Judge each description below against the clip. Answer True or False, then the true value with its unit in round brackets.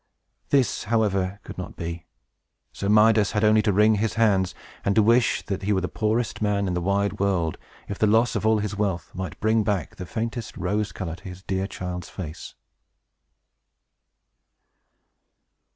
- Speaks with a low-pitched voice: True (100 Hz)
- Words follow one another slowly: False (170 wpm)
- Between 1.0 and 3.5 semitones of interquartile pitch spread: True (2.5 semitones)